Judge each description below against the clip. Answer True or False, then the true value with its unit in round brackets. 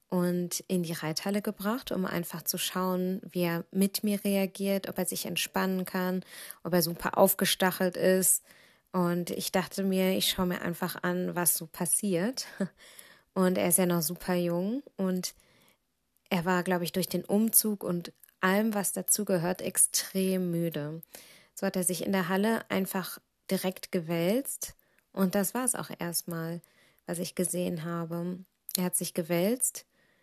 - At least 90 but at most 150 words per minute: False (165 wpm)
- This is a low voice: False (185 Hz)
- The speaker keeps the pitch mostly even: True (1.8 semitones)